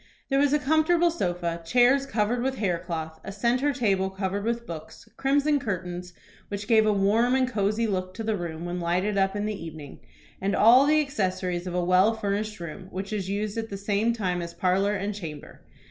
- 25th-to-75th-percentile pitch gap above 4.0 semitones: Yes, average, 4.4 semitones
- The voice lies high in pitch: Yes, high, 200 Hz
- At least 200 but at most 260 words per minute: Yes, fast, 205 wpm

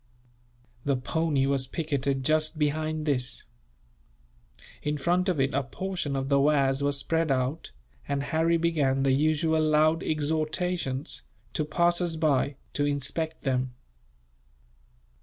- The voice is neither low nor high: Yes, medium, 150 Hz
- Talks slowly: Yes, slow, 125 wpm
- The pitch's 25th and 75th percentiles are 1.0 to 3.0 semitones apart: Yes, average, 2.7 semitones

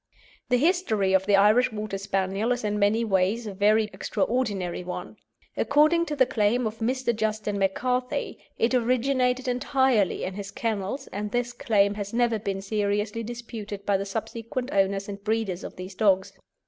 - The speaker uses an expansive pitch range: No, average, 3.5 semitones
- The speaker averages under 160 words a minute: No, average, 165 wpm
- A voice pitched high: Yes, high, 215 Hz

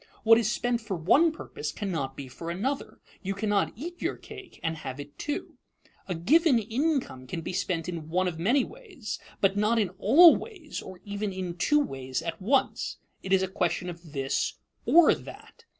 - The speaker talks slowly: No, average, 190 wpm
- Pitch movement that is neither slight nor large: No, wide, 8.1 semitones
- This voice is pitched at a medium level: No, high, 195 Hz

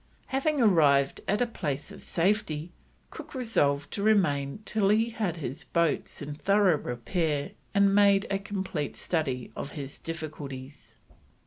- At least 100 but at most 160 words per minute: Yes, average, 145 wpm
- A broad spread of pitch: Yes, wide, 6.1 semitones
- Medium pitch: Yes, medium, 170 Hz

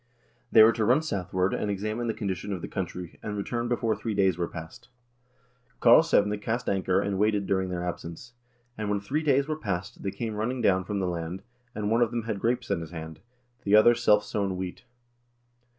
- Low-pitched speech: Yes, low, 105 Hz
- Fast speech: Yes, fast, 210 wpm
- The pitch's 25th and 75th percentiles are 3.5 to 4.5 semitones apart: Yes, average, 3.8 semitones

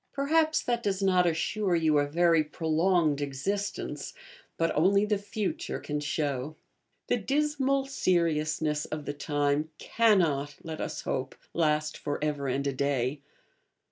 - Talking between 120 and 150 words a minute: Yes, average, 140 wpm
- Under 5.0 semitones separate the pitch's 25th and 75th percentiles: No, wide, 5.4 semitones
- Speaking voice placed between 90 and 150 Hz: No, medium, 160 Hz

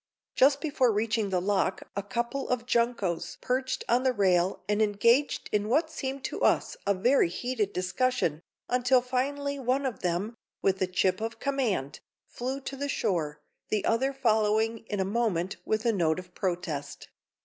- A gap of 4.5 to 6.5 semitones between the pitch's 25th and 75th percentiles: Yes, average, 5.2 semitones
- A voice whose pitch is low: No, high, 225 Hz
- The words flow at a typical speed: Yes, average, 170 wpm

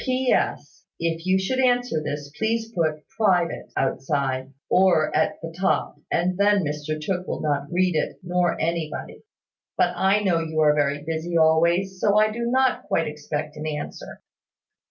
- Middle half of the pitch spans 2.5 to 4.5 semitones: Yes, average, 4.1 semitones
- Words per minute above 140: Yes, average, 160 wpm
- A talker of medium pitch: Yes, medium, 170 Hz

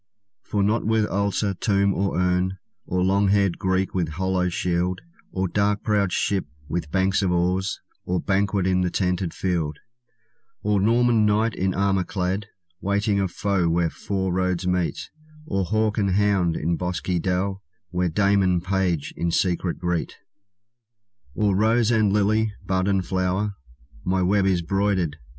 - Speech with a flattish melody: Yes, narrow, 1.9 semitones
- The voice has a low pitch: Yes, very low, 95 Hz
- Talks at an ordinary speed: Yes, average, 155 wpm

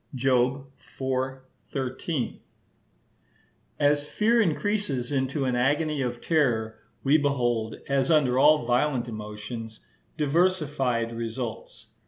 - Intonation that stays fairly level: No, average, 3.5 semitones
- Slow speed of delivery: Yes, slow, 100 wpm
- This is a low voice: Yes, low, 130 Hz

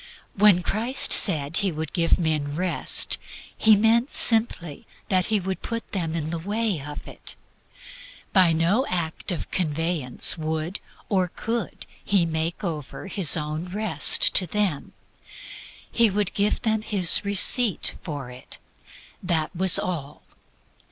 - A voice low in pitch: No, medium, 180 Hz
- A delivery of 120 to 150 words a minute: Yes, average, 140 wpm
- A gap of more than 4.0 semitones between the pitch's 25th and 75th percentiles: Yes, average, 4.5 semitones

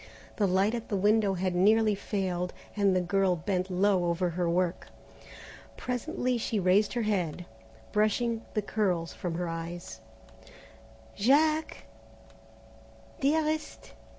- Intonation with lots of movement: No, average, 3.7 semitones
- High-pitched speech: Yes, high, 195 Hz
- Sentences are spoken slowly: Yes, slow, 125 wpm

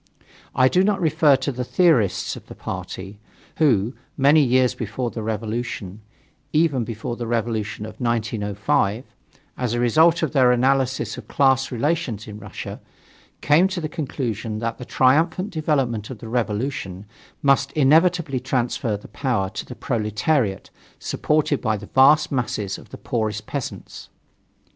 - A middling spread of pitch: Yes, average, 4.7 semitones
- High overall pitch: No, low, 125 Hz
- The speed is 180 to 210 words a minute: No, average, 150 wpm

